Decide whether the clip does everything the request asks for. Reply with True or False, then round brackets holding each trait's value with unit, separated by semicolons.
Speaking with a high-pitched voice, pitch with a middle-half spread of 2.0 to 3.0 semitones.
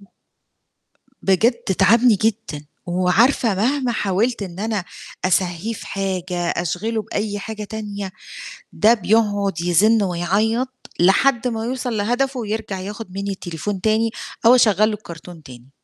False (205 Hz; 3.5 semitones)